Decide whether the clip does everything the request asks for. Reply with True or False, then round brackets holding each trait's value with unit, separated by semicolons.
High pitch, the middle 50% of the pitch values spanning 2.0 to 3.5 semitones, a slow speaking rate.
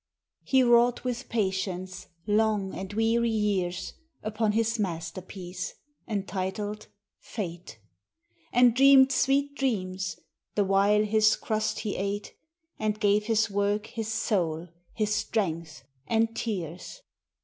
True (210 Hz; 3.1 semitones; 115 wpm)